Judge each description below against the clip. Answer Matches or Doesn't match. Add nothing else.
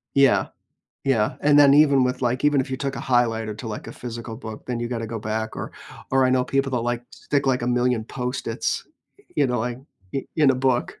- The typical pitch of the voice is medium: Doesn't match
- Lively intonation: Doesn't match